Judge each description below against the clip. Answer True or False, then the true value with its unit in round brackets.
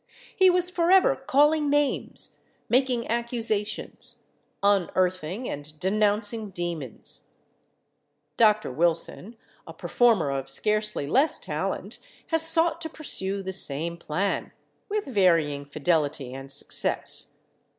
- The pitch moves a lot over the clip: True (8.0 semitones)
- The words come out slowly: True (105 wpm)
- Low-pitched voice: False (205 Hz)